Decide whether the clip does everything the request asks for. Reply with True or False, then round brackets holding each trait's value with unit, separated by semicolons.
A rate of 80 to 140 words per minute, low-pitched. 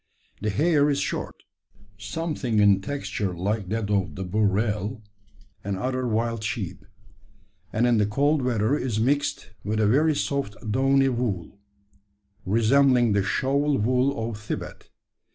True (135 wpm; 115 Hz)